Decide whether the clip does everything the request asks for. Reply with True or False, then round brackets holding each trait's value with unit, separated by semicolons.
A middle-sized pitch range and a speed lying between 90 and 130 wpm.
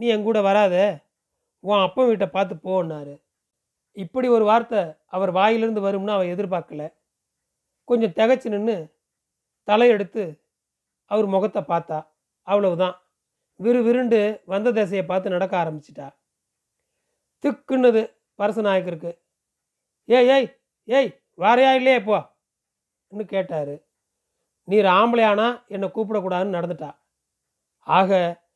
True (4.0 semitones; 100 wpm)